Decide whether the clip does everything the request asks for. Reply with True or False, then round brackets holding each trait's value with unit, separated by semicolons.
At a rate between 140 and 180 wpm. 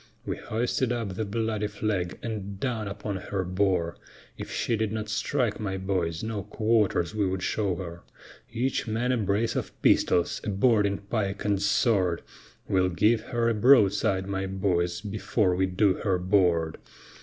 True (165 wpm)